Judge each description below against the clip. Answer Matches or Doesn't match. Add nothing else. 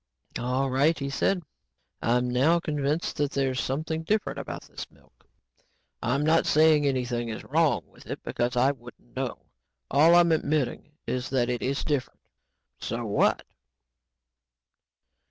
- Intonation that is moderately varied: Matches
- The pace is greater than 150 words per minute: Doesn't match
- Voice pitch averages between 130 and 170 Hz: Matches